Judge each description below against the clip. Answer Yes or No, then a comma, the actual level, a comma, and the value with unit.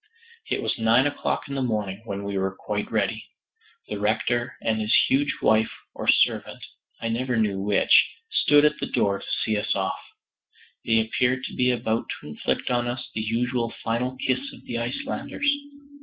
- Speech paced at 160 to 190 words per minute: Yes, average, 180 wpm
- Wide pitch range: No, average, 2.9 semitones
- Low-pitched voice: Yes, low, 115 Hz